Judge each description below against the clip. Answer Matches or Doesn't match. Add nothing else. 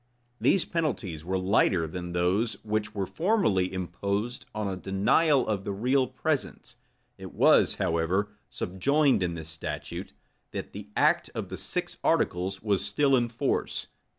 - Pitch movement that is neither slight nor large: Matches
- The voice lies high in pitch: Doesn't match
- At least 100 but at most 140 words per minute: Doesn't match